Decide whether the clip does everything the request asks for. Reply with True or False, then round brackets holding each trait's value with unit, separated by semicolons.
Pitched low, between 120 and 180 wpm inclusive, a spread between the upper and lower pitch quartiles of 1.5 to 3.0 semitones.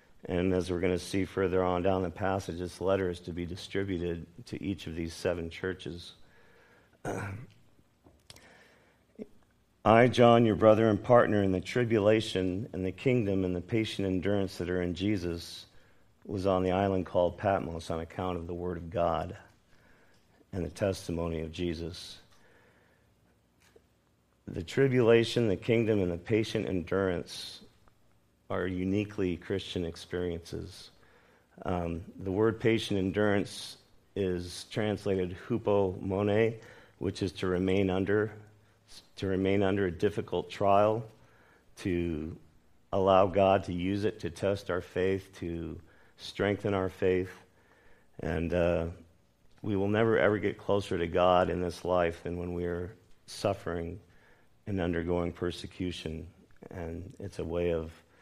True (95 Hz; 140 wpm; 2.7 semitones)